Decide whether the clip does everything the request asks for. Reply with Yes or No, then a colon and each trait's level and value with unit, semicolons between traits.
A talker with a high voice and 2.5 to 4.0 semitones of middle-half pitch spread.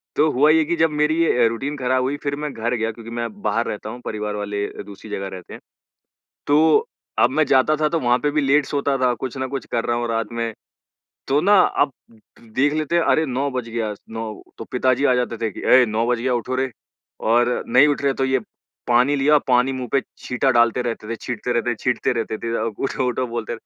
No: low, 125 Hz; average, 3.5 semitones